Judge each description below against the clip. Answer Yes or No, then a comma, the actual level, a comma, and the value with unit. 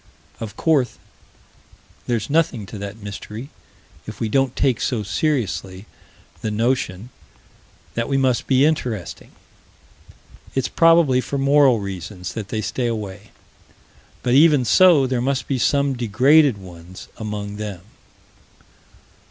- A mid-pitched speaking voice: No, low, 120 Hz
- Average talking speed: No, slow, 125 wpm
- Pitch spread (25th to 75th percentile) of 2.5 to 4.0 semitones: No, average, 4.8 semitones